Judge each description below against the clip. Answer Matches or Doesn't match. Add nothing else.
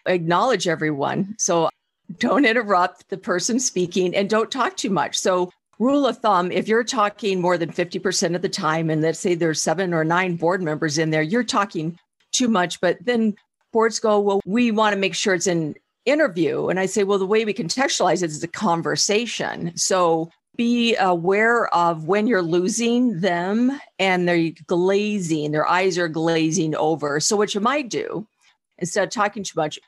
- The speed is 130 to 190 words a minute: Matches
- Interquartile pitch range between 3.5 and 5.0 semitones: Matches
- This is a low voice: Doesn't match